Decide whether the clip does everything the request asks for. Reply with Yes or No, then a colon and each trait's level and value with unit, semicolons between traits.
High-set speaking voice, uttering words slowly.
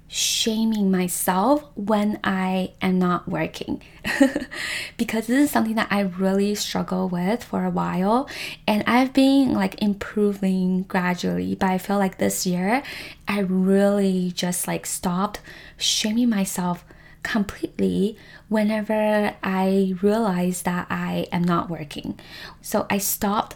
Yes: high, 195 Hz; slow, 125 wpm